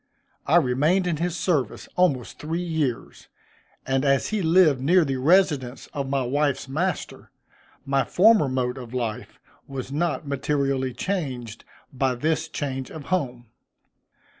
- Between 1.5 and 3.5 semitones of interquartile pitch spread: No, average, 4.2 semitones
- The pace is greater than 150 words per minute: No, average, 140 wpm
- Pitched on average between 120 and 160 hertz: Yes, medium, 140 Hz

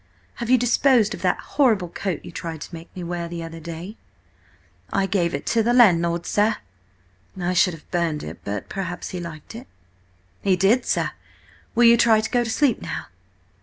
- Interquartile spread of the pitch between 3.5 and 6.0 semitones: Yes, average, 5.2 semitones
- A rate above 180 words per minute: Yes, average, 195 wpm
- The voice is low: No, medium, 185 Hz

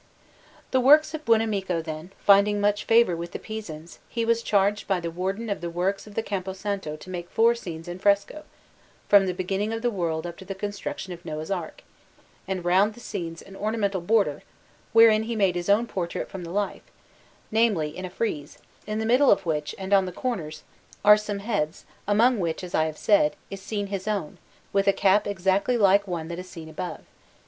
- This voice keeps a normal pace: No, fast, 210 wpm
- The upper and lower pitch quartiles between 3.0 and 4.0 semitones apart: Yes, average, 3.5 semitones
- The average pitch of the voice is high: Yes, high, 195 Hz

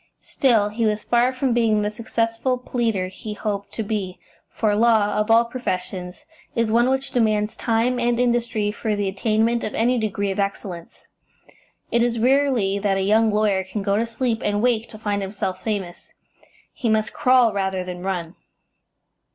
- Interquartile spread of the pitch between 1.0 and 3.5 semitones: Yes, average, 2.8 semitones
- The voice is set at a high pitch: Yes, high, 215 Hz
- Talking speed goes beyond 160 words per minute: Yes, average, 175 wpm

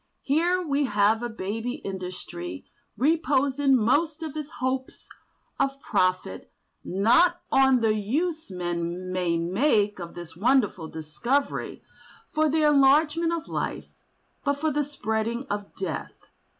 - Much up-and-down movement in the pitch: Yes, wide, 7.6 semitones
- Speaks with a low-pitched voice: No, very high, 250 Hz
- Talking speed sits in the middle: No, slow, 125 wpm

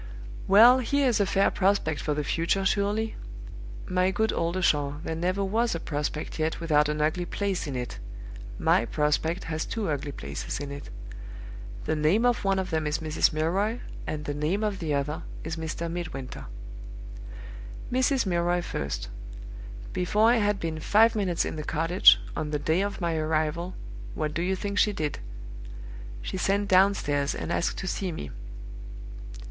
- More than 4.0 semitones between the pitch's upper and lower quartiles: Yes, average, 4.6 semitones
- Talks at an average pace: Yes, average, 170 wpm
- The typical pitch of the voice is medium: Yes, medium, 170 Hz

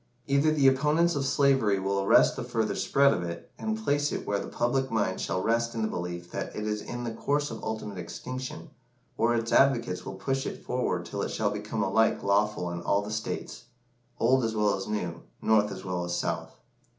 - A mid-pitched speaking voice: No, low, 110 Hz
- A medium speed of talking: No, fast, 210 wpm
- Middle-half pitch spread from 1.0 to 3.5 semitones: No, average, 5.2 semitones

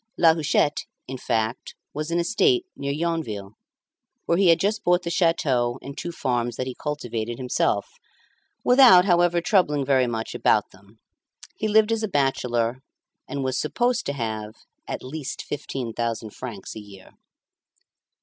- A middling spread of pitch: No, wide, 6.4 semitones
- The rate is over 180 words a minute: No, average, 155 wpm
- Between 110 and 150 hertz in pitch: Yes, medium, 140 Hz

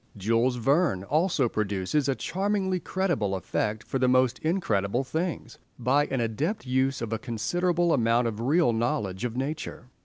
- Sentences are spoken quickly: No, average, 155 wpm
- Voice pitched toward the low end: Yes, low, 130 Hz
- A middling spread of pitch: No, wide, 5.8 semitones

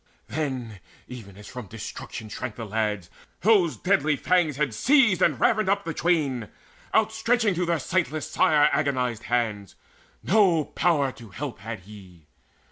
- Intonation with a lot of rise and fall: Yes, wide, 8.0 semitones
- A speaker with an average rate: Yes, average, 145 wpm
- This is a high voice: No, medium, 140 Hz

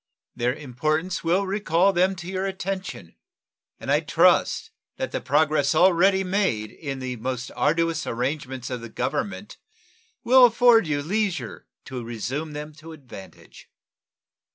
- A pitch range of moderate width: No, wide, 6.5 semitones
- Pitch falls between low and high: Yes, medium, 160 Hz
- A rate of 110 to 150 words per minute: Yes, slow, 135 wpm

